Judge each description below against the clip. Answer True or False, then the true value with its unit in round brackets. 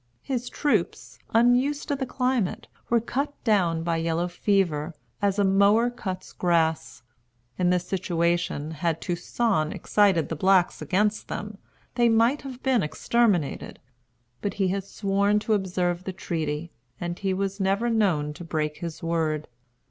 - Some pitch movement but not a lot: True (4.7 semitones)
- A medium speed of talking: True (150 wpm)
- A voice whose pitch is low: False (190 Hz)